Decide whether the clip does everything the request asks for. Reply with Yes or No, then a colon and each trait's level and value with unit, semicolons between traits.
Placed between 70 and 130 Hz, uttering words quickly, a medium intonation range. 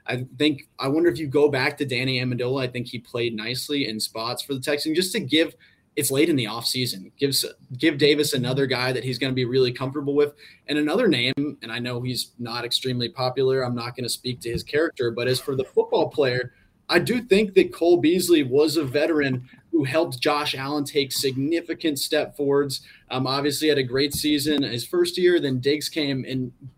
No: medium, 140 Hz; fast, 215 wpm; average, 3.2 semitones